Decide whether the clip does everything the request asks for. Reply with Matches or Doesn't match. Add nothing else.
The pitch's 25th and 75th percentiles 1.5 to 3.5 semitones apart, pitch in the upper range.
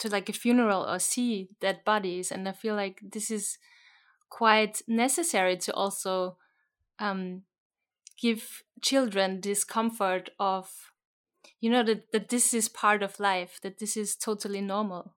Matches